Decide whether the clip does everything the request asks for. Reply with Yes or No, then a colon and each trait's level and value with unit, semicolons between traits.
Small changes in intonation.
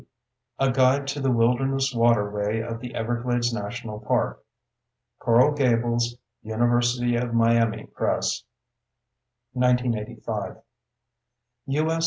Yes: narrow, 1.7 semitones